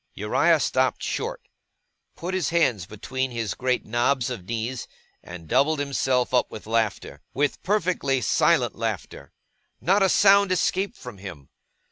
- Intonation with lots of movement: Yes, wide, 7.3 semitones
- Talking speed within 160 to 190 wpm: No, average, 140 wpm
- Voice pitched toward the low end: Yes, low, 130 Hz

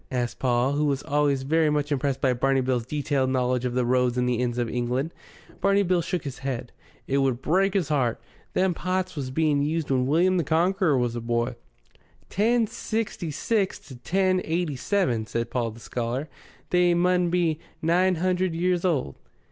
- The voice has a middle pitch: Yes, medium, 145 Hz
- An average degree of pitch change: No, wide, 5.9 semitones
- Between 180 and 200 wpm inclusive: Yes, average, 190 wpm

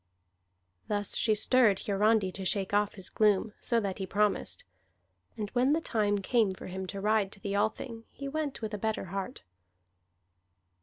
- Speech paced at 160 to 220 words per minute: Yes, average, 170 wpm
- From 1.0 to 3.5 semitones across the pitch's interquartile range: Yes, narrow, 2.4 semitones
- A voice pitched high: Yes, high, 210 Hz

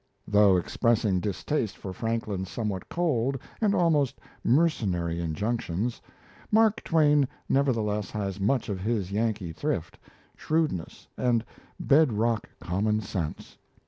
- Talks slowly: Yes, slow, 110 wpm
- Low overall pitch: Yes, low, 110 Hz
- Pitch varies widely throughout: Yes, wide, 5.9 semitones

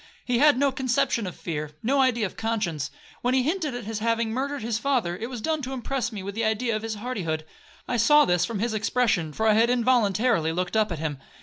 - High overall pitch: Yes, high, 225 Hz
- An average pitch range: Yes, average, 4.2 semitones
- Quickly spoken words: Yes, fast, 230 wpm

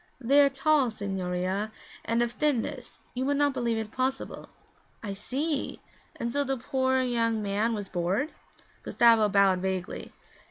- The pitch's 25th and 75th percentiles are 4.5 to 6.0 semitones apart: Yes, average, 4.8 semitones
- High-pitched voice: Yes, high, 235 Hz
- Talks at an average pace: Yes, average, 155 wpm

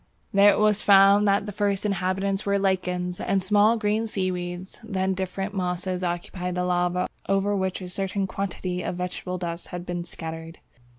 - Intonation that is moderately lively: No, narrow, 1.8 semitones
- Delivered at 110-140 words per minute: No, average, 170 wpm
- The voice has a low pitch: No, high, 190 Hz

